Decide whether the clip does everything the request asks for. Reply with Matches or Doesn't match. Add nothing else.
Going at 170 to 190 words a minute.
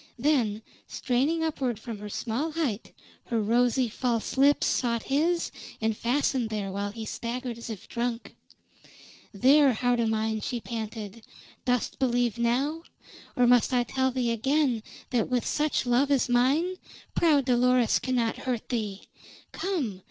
Doesn't match